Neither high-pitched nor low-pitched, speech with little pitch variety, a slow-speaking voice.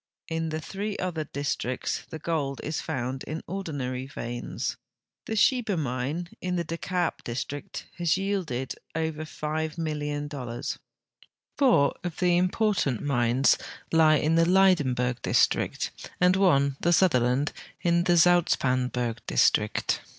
No: medium, 155 Hz; average, 4.9 semitones; slow, 130 wpm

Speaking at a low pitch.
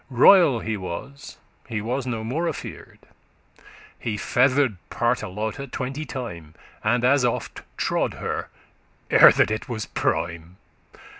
Yes: low, 120 Hz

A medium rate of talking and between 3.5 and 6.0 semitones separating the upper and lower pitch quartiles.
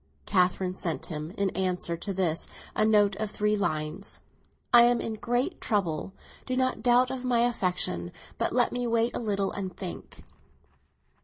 Yes: average, 165 wpm; average, 4.7 semitones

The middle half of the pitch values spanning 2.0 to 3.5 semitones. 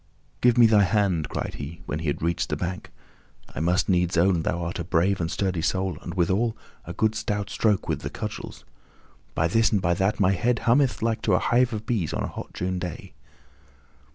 No: average, 4.1 semitones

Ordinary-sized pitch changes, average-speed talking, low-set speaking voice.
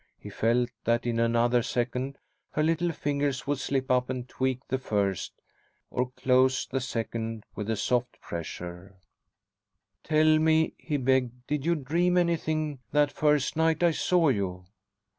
Yes: average, 4.4 semitones; average, 150 wpm; low, 130 Hz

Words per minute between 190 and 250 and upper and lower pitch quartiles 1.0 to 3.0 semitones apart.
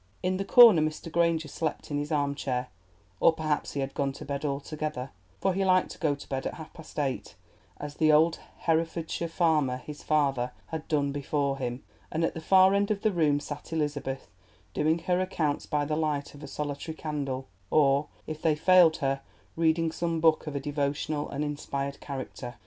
Yes: average, 195 wpm; narrow, 2.5 semitones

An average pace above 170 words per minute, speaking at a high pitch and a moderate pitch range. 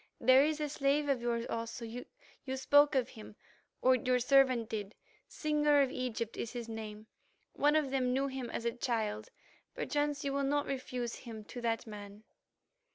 No: average, 165 wpm; very high, 255 Hz; average, 3.3 semitones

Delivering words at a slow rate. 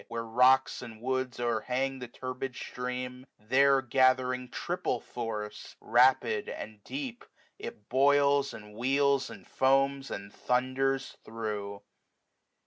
Yes: slow, 120 wpm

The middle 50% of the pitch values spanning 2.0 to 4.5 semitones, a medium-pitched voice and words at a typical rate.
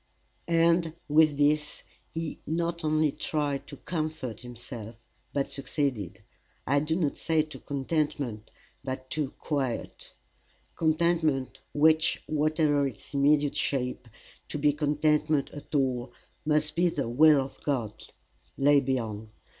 No: average, 2.7 semitones; medium, 145 Hz; slow, 120 wpm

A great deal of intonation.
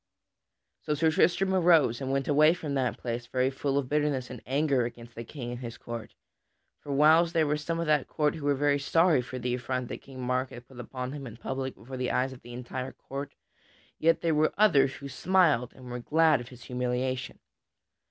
No: average, 3.3 semitones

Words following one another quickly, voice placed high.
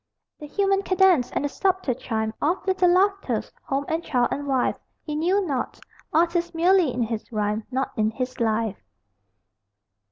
No: average, 160 wpm; very high, 290 Hz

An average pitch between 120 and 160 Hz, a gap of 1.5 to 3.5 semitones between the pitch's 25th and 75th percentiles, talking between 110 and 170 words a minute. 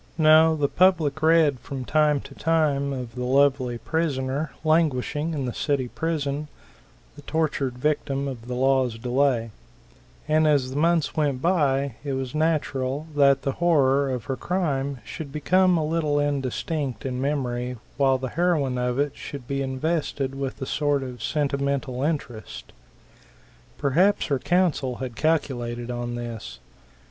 Yes: medium, 140 Hz; average, 3.2 semitones; average, 150 wpm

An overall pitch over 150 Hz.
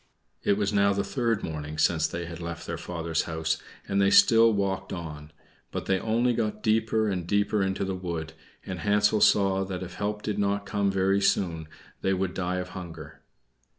No: very low, 95 Hz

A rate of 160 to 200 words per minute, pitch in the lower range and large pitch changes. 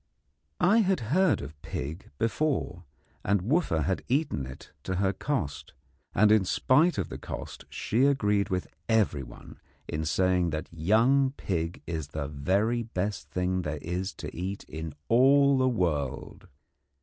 No: average, 150 wpm; very low, 95 Hz; wide, 7.8 semitones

